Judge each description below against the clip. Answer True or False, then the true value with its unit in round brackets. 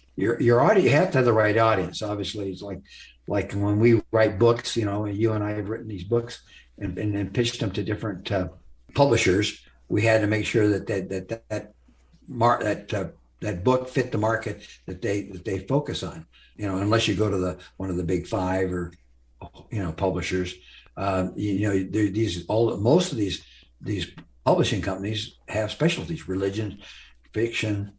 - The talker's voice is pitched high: False (105 Hz)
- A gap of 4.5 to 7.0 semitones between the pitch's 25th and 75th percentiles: False (3.0 semitones)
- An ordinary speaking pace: True (195 wpm)